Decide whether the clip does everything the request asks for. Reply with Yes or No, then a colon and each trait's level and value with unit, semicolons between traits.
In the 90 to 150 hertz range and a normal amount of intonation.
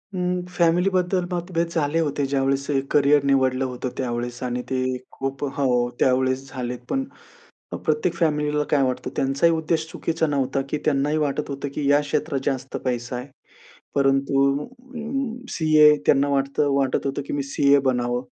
Yes: medium, 140 Hz; average, 3.0 semitones